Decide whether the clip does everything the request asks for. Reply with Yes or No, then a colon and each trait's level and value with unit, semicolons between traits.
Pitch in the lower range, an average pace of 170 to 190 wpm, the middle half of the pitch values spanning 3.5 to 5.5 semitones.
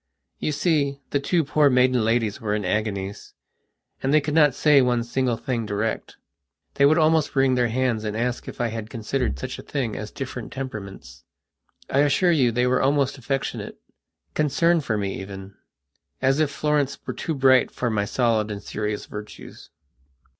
Yes: low, 125 Hz; average, 175 wpm; average, 4.5 semitones